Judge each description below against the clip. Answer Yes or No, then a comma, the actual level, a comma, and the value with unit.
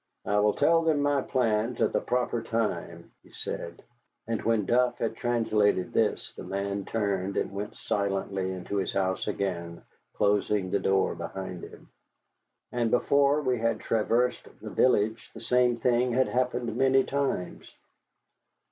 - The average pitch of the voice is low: Yes, low, 115 Hz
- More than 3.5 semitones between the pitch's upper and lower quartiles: Yes, average, 3.9 semitones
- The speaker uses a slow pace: No, average, 150 wpm